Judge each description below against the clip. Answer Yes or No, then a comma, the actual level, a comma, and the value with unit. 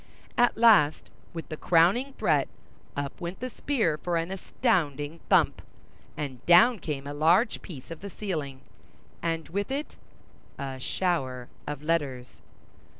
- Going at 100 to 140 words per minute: Yes, slow, 135 wpm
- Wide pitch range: Yes, wide, 5.7 semitones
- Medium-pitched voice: Yes, medium, 165 Hz